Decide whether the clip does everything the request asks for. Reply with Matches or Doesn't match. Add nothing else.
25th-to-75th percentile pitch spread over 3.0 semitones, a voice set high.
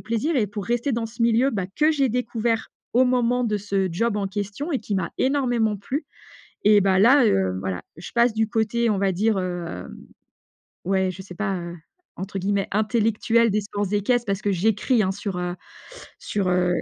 Matches